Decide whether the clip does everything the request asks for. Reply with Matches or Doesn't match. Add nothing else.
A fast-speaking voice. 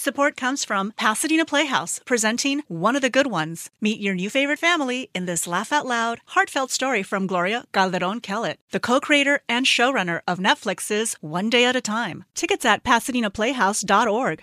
Doesn't match